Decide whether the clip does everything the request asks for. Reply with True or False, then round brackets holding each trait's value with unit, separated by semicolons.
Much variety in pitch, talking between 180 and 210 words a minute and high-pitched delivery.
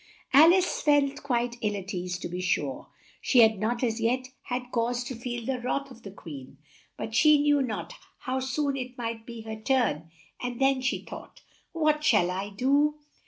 False (3.8 semitones; 195 wpm; 245 Hz)